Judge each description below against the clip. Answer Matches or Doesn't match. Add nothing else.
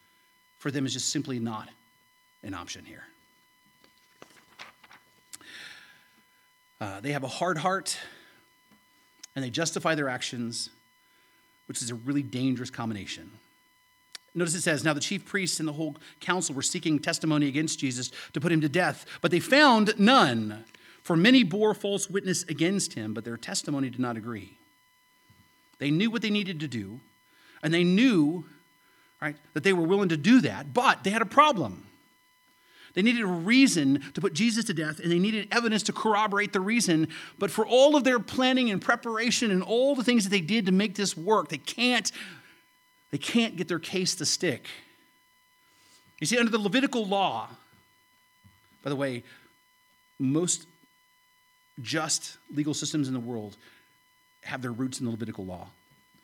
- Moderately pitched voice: Matches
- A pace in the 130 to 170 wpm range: Matches